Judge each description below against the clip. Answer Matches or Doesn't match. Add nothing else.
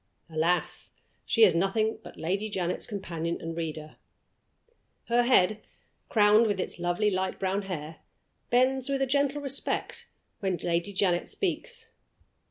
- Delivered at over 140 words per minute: Doesn't match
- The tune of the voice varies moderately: Doesn't match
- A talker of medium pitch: Doesn't match